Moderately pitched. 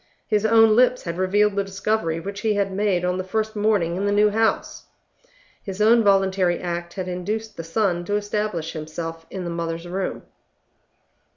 No: high, 195 Hz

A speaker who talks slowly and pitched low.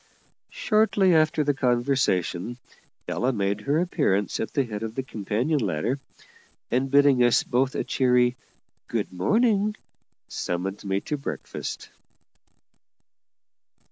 Yes: slow, 115 wpm; low, 125 Hz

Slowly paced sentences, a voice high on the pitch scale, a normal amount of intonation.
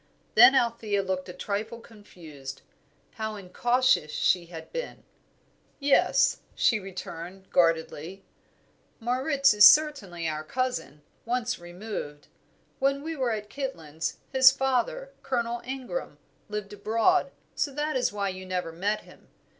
No: slow, 125 wpm; high, 215 Hz; wide, 6.2 semitones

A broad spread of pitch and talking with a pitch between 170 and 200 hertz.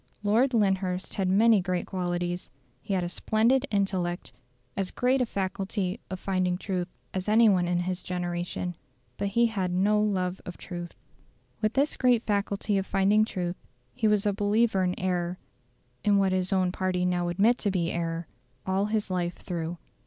No: narrow, 2.6 semitones; high, 190 Hz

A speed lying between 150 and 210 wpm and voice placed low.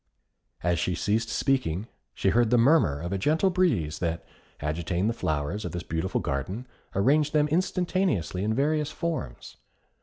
Yes: average, 155 wpm; low, 105 Hz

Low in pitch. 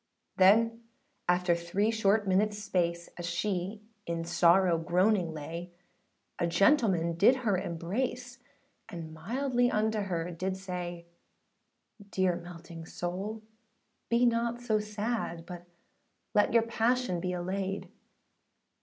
No: high, 190 Hz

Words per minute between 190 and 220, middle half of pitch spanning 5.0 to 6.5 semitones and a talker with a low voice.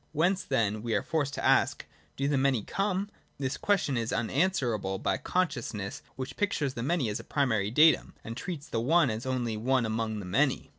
Yes: fast, 205 wpm; wide, 5.4 semitones; low, 130 Hz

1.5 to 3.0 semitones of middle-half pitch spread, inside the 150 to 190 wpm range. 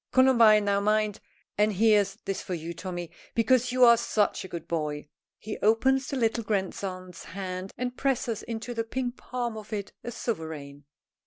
No: average, 4.3 semitones; average, 170 wpm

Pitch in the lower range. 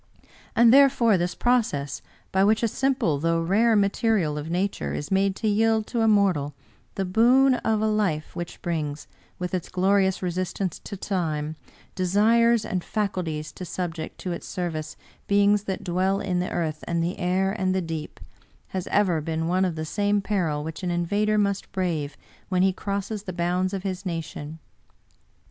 No: medium, 185 Hz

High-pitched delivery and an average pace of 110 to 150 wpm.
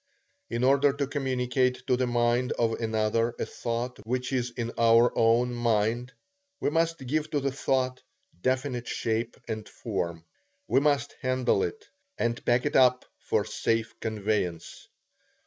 No: low, 125 Hz; average, 145 wpm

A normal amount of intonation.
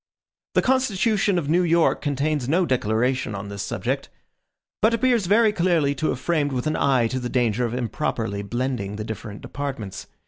No: wide, 6.8 semitones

